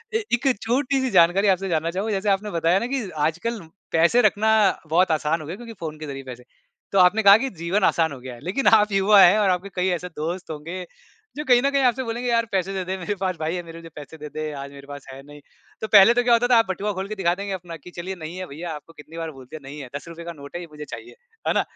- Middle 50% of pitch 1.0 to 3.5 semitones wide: No, average, 4.7 semitones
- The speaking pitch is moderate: Yes, medium, 180 Hz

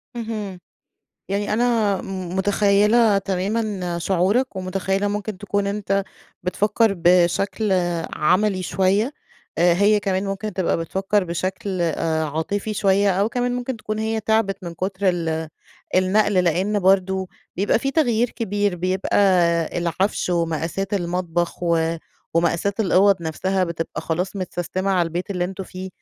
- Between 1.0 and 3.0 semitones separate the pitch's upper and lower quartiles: Yes, narrow, 2.5 semitones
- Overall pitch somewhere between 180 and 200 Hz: Yes, high, 190 Hz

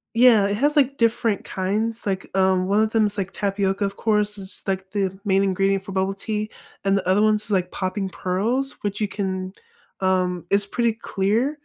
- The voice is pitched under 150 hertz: No, high, 200 Hz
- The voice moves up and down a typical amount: No, narrow, 2.2 semitones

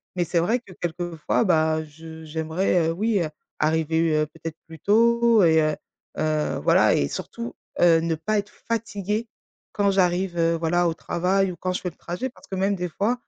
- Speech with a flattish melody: No, average, 3.8 semitones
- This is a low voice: No, medium, 175 Hz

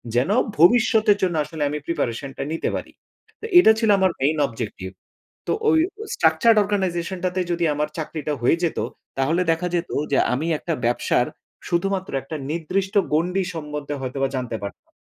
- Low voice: No, medium, 165 Hz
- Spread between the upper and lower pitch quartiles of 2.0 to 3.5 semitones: No, average, 4.7 semitones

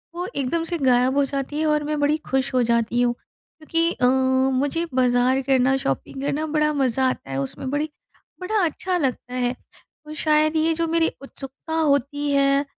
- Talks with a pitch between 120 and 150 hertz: No, very high, 280 Hz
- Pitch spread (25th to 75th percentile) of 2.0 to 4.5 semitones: Yes, average, 3.3 semitones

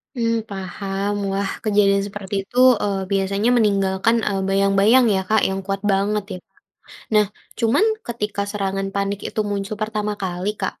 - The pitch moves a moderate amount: No, narrow, 1.4 semitones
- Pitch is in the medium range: No, high, 200 Hz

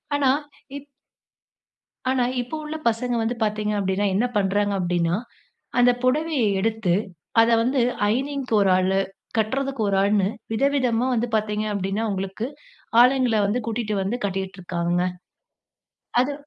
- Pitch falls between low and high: No, high, 220 Hz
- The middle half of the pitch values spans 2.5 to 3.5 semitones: No, average, 4.4 semitones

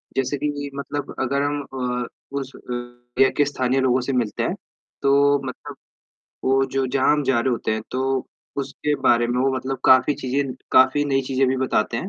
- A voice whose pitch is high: No, low, 130 Hz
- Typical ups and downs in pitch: No, narrow, 1.8 semitones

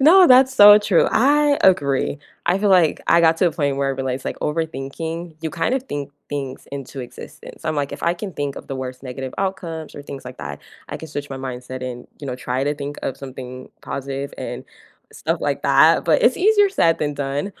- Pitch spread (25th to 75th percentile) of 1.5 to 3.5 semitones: No, average, 5.0 semitones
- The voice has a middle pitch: Yes, medium, 145 Hz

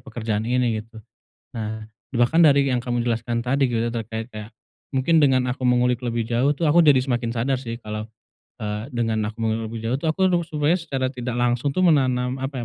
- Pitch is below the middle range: Yes, low, 125 Hz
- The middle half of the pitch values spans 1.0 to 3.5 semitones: Yes, average, 2.9 semitones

